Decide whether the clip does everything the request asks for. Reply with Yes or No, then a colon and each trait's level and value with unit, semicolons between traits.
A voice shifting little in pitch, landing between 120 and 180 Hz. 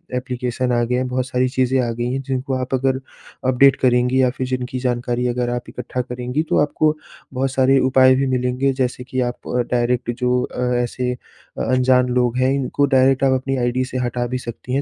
Yes: narrow, 1.0 semitones; low, 125 Hz